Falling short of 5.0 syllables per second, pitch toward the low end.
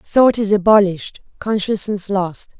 No: 4.4 syllables/s; high, 205 Hz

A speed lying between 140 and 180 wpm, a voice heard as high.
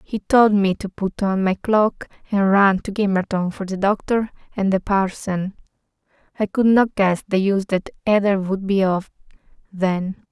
Yes: average, 175 wpm; high, 195 Hz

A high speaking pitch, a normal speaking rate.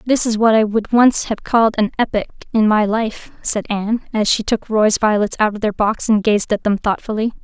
No: high, 215 Hz; fast, 235 wpm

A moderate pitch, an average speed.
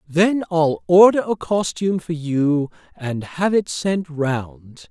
Yes: medium, 160 Hz; average, 145 wpm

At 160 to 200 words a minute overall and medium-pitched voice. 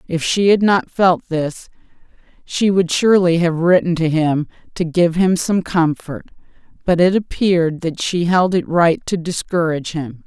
Yes: average, 170 wpm; medium, 170 Hz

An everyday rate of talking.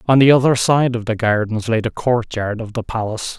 No: fast, 230 wpm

